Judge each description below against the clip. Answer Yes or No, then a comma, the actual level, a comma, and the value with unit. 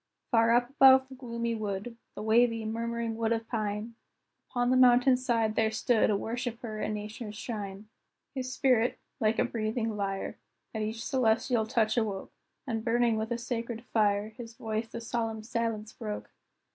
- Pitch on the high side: Yes, high, 225 Hz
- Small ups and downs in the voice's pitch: Yes, narrow, 1.8 semitones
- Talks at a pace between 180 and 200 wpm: No, average, 165 wpm